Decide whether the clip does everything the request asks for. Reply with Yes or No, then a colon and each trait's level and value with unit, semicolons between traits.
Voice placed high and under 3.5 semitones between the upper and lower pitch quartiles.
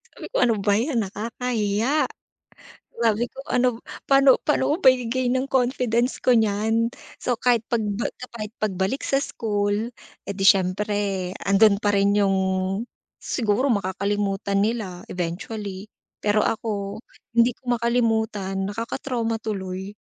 Yes: high, 220 Hz; average, 3.1 semitones